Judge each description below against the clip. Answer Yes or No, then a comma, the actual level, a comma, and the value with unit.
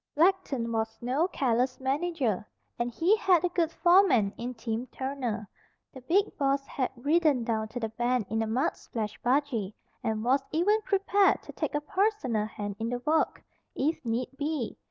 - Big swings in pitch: Yes, wide, 6.2 semitones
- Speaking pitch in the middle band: No, very high, 260 Hz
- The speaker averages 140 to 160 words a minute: No, average, 175 wpm